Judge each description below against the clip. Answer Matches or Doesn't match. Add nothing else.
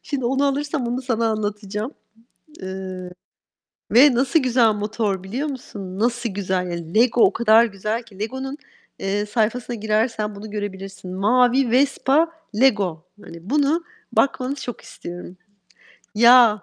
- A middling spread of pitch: Matches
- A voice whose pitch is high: Matches